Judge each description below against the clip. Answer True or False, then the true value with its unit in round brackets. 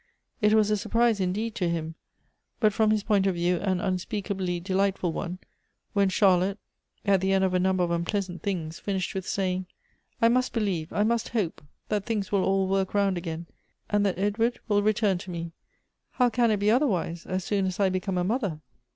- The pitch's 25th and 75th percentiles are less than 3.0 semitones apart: True (2.6 semitones)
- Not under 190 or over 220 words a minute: True (205 wpm)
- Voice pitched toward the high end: True (195 Hz)